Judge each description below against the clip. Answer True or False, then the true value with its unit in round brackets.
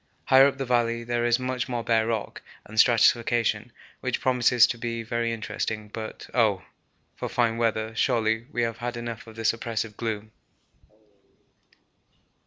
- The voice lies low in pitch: True (115 Hz)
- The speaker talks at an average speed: True (155 wpm)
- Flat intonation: True (1.2 semitones)